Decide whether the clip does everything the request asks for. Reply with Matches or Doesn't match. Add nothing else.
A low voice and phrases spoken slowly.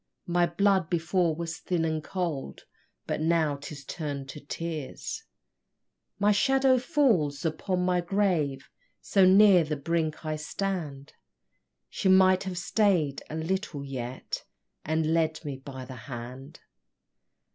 Doesn't match